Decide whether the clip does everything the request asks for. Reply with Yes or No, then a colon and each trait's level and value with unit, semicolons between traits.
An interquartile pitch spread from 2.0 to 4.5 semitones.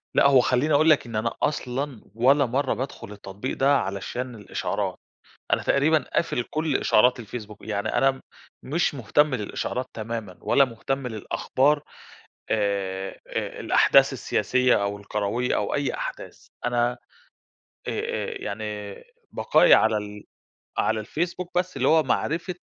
No: average, 5.0 semitones